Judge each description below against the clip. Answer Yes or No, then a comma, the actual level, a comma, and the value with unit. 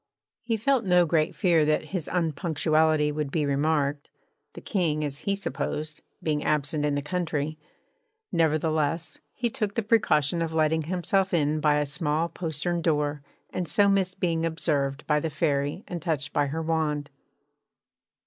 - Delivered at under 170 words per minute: Yes, average, 160 wpm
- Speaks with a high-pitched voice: No, medium, 155 Hz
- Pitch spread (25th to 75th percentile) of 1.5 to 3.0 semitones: Yes, average, 2.7 semitones